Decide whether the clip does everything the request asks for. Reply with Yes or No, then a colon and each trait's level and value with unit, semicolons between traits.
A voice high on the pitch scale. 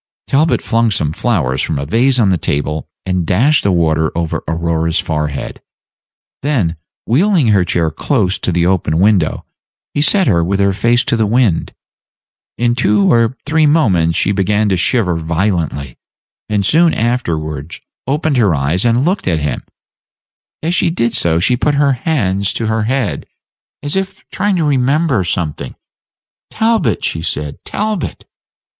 No: low, 105 Hz